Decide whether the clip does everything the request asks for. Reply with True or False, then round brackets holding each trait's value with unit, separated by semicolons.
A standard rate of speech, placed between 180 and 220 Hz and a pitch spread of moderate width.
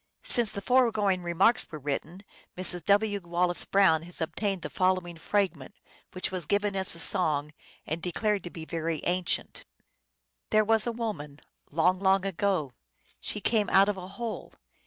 True (165 wpm; 185 Hz; 3.4 semitones)